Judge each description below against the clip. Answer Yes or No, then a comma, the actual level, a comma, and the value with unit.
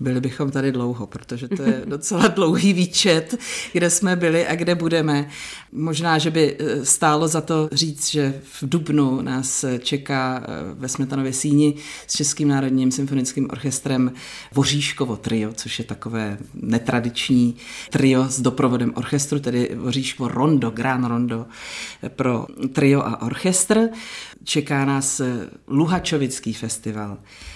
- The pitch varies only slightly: No, average, 3.7 semitones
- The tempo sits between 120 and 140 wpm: Yes, average, 130 wpm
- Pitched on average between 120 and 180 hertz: Yes, low, 135 Hz